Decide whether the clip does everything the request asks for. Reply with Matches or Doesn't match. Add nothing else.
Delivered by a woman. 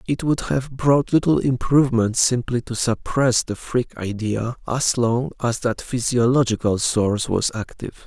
Doesn't match